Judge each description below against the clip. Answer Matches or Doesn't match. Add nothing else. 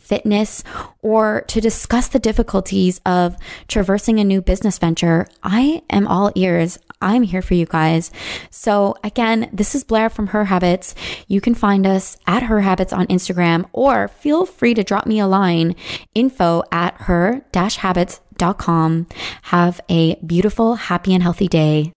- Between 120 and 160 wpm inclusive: Matches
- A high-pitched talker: Matches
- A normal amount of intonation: Matches